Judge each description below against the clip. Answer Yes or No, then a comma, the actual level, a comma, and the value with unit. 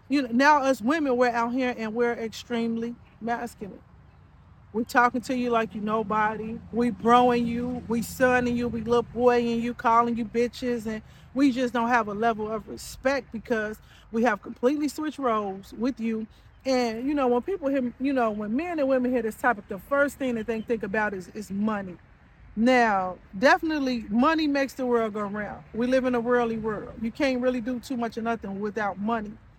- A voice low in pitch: No, high, 235 Hz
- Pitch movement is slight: Yes, narrow, 2.3 semitones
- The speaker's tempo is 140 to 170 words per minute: No, average, 200 wpm